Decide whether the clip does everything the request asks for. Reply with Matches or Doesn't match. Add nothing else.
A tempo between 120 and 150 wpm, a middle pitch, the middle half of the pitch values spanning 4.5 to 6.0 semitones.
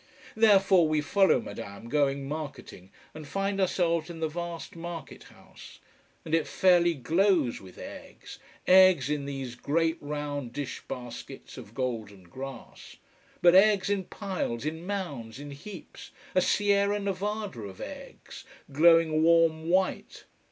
Matches